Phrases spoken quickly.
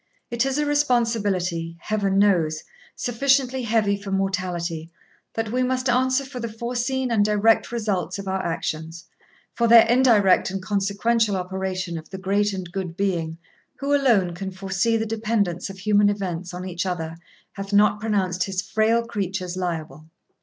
No: average, 155 wpm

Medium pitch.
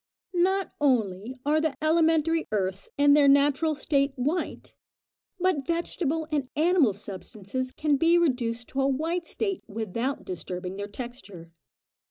No: very high, 275 Hz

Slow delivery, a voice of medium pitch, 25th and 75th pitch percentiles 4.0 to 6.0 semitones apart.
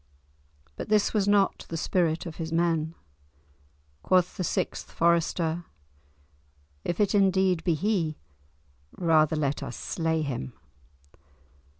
No: slow, 115 wpm; medium, 170 Hz; average, 2.8 semitones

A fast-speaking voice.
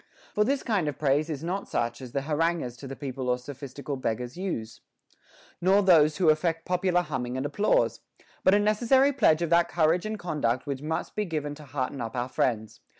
Yes: fast, 210 wpm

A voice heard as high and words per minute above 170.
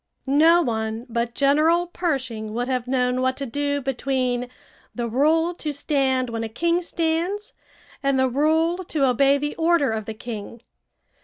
No: very high, 270 Hz; average, 160 wpm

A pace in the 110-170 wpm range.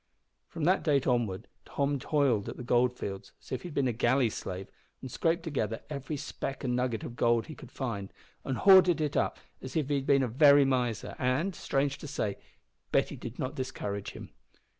No: fast, 205 wpm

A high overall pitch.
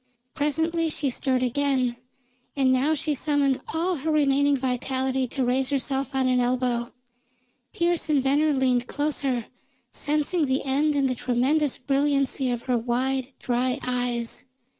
Yes: very high, 270 Hz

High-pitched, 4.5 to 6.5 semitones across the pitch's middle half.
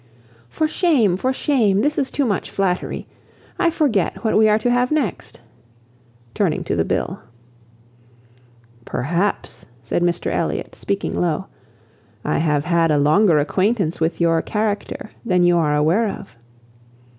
Yes: high, 195 Hz; wide, 5.6 semitones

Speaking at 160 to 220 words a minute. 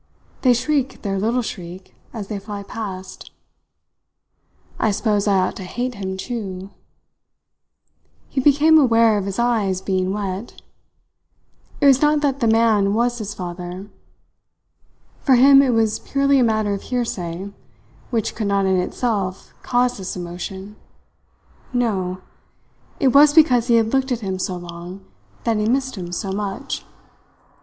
No: average, 150 wpm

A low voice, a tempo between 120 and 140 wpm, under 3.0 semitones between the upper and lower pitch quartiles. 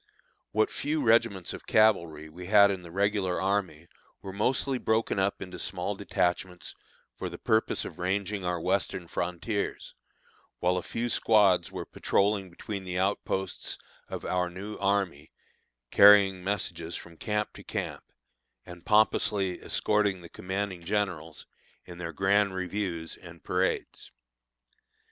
Yes: very low, 95 Hz; slow, 135 wpm; narrow, 2.6 semitones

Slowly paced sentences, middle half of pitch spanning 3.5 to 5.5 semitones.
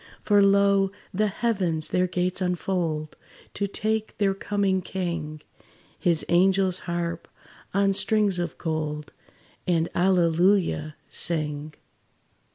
No: slow, 105 wpm; average, 3.1 semitones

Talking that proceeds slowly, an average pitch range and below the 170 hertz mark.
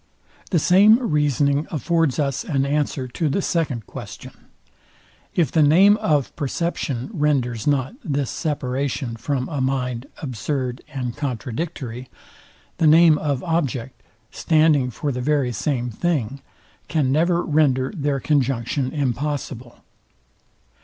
Yes: slow, 120 wpm; average, 3.5 semitones; medium, 140 Hz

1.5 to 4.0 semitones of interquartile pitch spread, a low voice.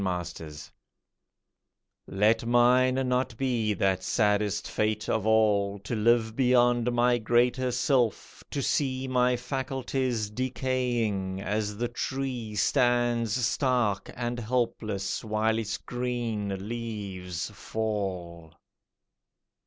Yes: average, 3.1 semitones; low, 115 Hz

